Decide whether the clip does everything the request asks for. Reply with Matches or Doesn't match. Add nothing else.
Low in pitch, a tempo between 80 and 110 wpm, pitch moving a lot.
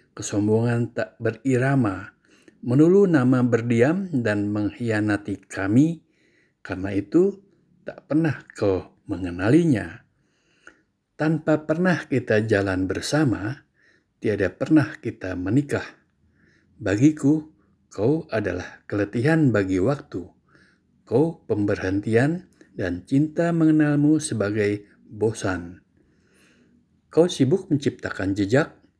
Matches